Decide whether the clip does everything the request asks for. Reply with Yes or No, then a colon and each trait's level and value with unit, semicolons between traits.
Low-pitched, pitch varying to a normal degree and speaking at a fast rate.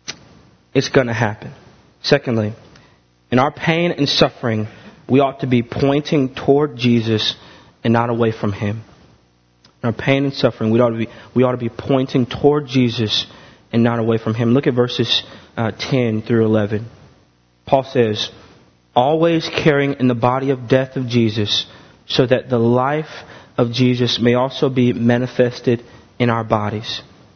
No: low, 120 Hz; average, 3.0 semitones; average, 160 wpm